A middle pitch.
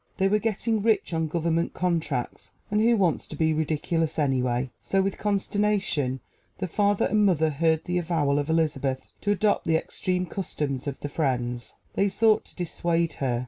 Yes: medium, 165 Hz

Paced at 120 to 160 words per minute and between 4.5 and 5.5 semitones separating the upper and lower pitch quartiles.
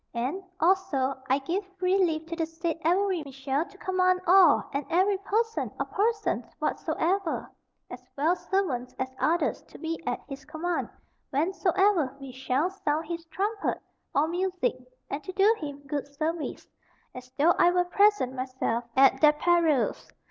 Yes: average, 155 wpm; average, 5.1 semitones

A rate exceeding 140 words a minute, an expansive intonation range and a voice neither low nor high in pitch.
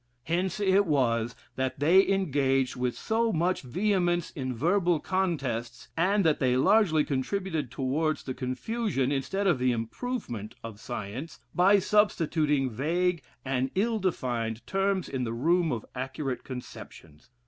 No: slow, 135 wpm; wide, 6.7 semitones; medium, 150 Hz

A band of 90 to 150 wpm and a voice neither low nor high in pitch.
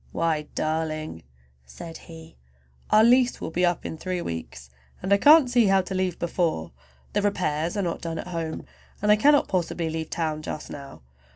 No: average, 185 wpm; medium, 170 Hz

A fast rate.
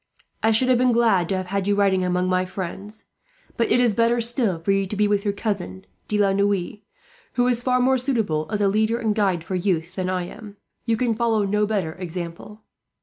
Yes: fast, 225 wpm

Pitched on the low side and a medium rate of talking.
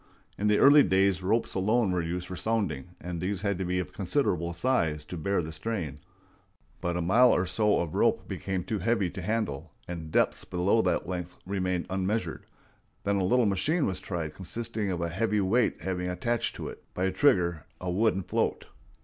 Yes: very low, 95 Hz; average, 195 wpm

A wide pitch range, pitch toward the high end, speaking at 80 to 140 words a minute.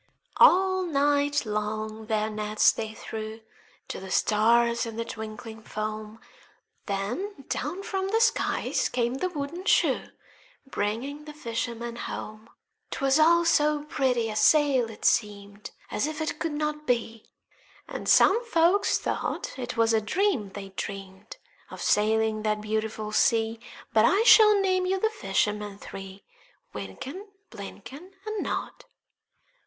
Yes: wide, 6.2 semitones; high, 235 Hz; slow, 135 wpm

